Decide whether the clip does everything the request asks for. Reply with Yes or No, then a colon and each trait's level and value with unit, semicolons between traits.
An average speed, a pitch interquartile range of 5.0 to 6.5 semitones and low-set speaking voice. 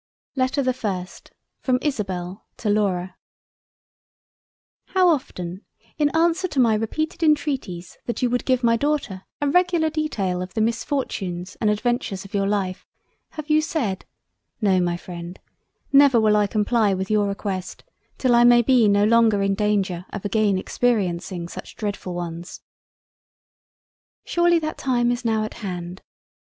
No: average, 150 wpm; wide, 5.5 semitones; high, 215 Hz